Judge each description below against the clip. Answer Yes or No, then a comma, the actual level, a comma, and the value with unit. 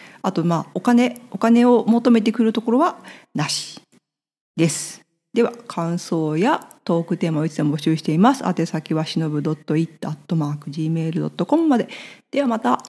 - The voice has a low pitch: No, medium, 170 Hz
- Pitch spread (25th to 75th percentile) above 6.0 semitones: Yes, wide, 6.8 semitones